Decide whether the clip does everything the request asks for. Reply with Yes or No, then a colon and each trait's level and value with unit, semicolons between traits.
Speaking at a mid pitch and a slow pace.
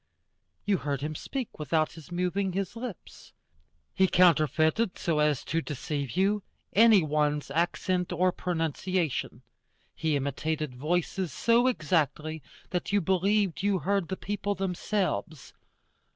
Yes: medium, 175 Hz; slow, 125 wpm